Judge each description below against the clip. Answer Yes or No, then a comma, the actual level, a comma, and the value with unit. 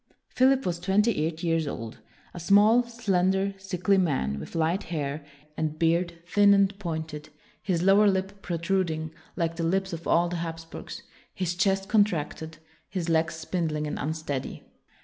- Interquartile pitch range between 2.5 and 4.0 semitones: Yes, average, 3.3 semitones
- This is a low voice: No, medium, 170 Hz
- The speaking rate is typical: Yes, average, 155 wpm